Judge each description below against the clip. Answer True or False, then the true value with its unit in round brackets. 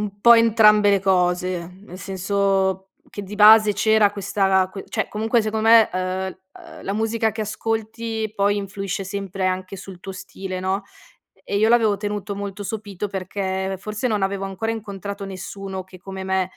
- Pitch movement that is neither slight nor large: False (2.0 semitones)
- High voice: True (200 Hz)